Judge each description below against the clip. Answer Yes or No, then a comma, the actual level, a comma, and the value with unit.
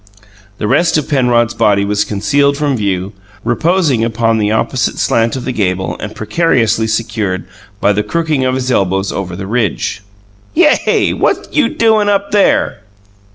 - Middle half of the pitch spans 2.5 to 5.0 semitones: No, wide, 5.4 semitones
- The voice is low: Yes, low, 115 Hz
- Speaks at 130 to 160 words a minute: Yes, average, 155 wpm